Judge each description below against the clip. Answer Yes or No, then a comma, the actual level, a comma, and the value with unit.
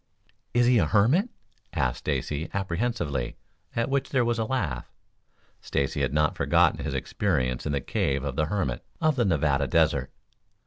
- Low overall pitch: Yes, very low, 80 Hz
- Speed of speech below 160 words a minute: No, average, 165 wpm